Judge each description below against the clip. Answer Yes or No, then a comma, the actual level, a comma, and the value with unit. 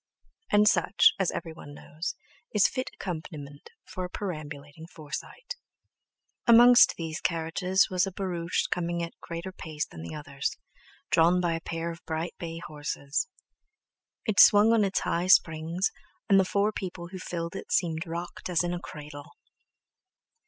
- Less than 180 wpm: Yes, average, 155 wpm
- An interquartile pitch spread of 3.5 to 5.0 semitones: No, average, 2.9 semitones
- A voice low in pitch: No, medium, 170 Hz